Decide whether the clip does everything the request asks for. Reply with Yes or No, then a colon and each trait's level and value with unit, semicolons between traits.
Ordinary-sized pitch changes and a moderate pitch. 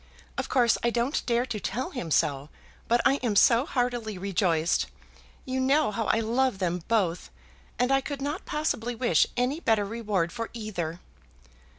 No: average, 4.6 semitones; high, 230 Hz